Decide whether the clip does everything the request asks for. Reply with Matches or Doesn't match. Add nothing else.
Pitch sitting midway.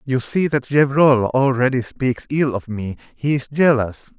Doesn't match